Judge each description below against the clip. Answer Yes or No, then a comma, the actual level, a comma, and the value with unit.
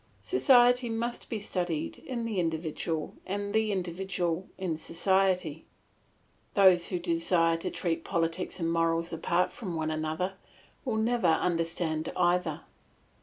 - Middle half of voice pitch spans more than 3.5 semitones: No, average, 3.2 semitones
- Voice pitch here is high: No, medium, 175 Hz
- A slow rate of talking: Yes, slow, 125 wpm